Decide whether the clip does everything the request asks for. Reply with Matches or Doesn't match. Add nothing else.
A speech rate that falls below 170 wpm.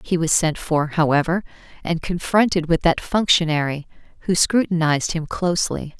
Matches